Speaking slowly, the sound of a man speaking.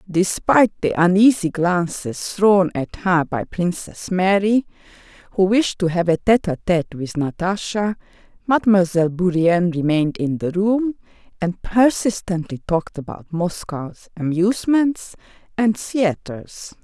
No: slow, 115 wpm; female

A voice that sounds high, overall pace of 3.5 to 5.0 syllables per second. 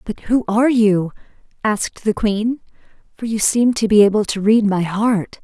Yes: high, 215 Hz; 4.7 syllables/s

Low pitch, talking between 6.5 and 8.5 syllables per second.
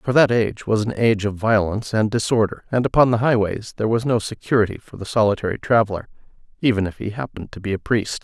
Yes: low, 110 Hz; 6.6 syllables/s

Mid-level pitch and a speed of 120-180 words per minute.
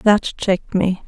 No: high, 195 Hz; average, 165 wpm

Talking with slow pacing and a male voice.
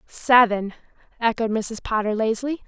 No: slow, 110 wpm; female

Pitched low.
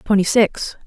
No: high, 205 Hz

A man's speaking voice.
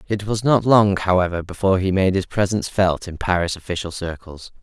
Yes: male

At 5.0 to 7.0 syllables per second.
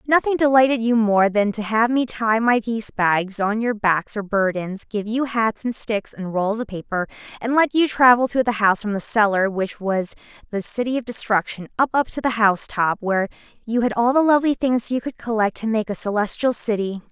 Yes: 5.3 syllables/s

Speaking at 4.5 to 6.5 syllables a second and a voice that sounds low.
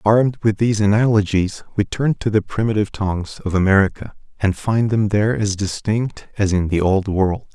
Yes: 5.4 syllables/s; low, 105 Hz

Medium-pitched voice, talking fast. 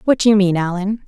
No: high, 200 Hz; fast, 280 wpm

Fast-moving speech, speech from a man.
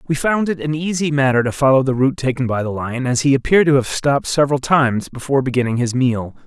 Yes: fast, 240 wpm; male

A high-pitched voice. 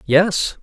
No: medium, 170 Hz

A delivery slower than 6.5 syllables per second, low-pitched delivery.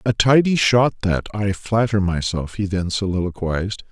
Yes: 4.7 syllables/s; low, 100 Hz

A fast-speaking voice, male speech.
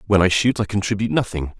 Yes: fast, 225 wpm; male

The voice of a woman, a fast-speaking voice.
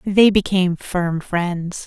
No: female; slow, 130 wpm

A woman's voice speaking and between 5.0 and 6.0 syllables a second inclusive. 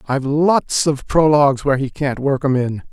No: male; 5.2 syllables/s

